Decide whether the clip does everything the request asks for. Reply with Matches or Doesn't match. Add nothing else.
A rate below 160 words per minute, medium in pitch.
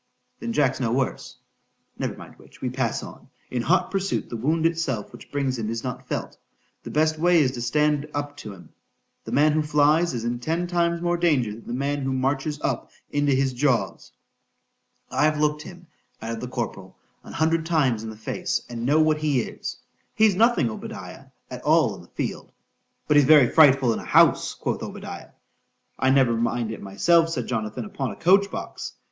Doesn't match